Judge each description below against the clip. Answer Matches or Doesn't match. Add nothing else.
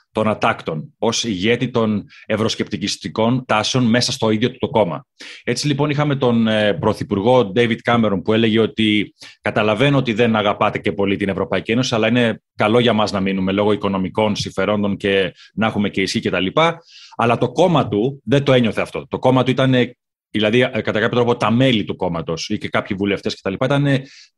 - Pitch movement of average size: Matches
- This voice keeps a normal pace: Doesn't match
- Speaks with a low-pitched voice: Matches